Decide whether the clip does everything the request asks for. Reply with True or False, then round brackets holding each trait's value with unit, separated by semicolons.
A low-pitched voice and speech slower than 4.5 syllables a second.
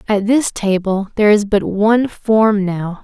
False (205 Hz; 4.3 syllables/s)